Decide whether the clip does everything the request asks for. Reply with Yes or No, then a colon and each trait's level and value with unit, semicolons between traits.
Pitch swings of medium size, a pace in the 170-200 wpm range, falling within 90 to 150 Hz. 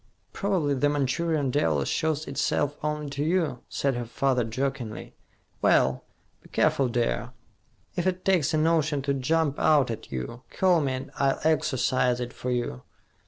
No: average, 3.9 semitones; average, 160 wpm; medium, 140 Hz